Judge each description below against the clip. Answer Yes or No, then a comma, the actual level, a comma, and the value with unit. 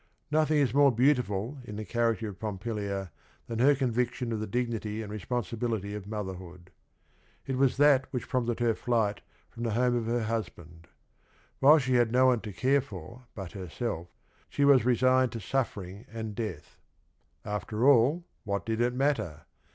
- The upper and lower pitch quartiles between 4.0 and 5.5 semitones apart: No, average, 3.6 semitones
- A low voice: Yes, low, 115 Hz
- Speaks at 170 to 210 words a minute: Yes, average, 175 wpm